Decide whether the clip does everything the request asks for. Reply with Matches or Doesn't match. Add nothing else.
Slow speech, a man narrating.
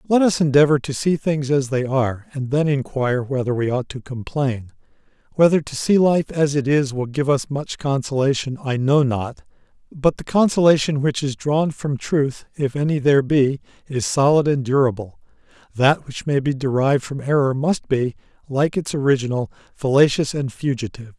Doesn't match